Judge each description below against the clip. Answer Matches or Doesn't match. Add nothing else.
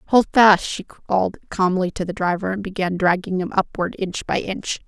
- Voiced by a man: Doesn't match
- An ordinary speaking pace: Matches